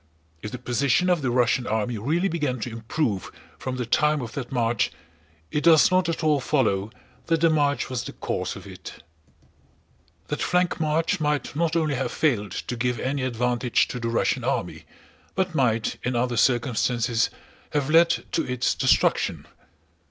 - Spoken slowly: No, average, 170 wpm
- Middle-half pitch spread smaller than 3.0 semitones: No, average, 4.6 semitones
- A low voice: Yes, low, 130 Hz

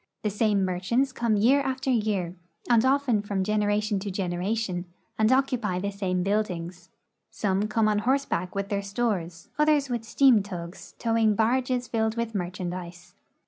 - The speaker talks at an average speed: Yes, average, 155 wpm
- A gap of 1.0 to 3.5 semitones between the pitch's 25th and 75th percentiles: No, average, 4.0 semitones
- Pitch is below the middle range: No, high, 210 Hz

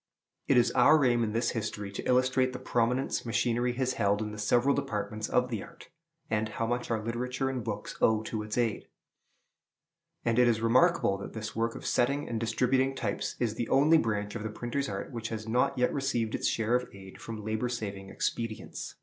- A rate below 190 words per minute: No, fast, 205 wpm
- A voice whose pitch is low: Yes, low, 115 Hz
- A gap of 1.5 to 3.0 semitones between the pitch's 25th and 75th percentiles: Yes, narrow, 2.6 semitones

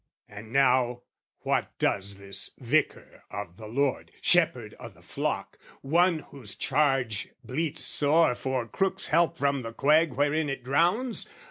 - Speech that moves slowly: No, average, 145 wpm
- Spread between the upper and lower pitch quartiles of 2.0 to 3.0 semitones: No, average, 5.2 semitones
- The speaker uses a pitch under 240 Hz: Yes, low, 135 Hz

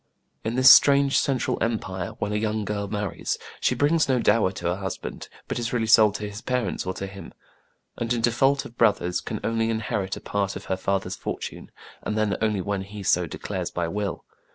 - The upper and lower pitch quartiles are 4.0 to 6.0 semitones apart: No, average, 3.0 semitones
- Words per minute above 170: Yes, fast, 205 wpm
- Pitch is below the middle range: Yes, low, 105 Hz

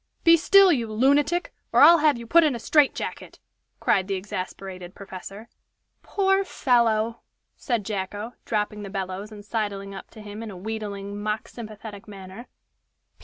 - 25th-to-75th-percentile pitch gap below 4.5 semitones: Yes, average, 3.6 semitones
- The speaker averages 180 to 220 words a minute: No, average, 160 wpm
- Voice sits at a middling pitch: No, high, 215 Hz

